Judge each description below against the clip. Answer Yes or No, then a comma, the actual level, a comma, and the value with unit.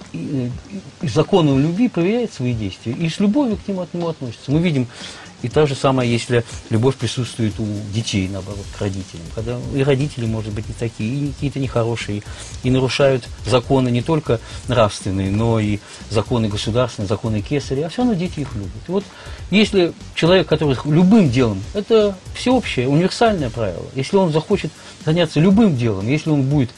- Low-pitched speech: Yes, low, 130 Hz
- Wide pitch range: Yes, wide, 6.3 semitones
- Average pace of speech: No, fast, 170 wpm